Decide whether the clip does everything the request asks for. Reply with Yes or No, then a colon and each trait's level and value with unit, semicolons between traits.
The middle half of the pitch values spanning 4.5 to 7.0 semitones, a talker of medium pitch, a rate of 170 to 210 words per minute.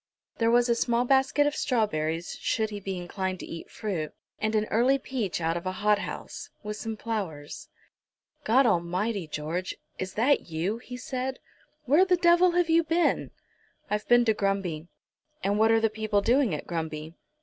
No: wide, 5.5 semitones; high, 215 Hz; average, 175 wpm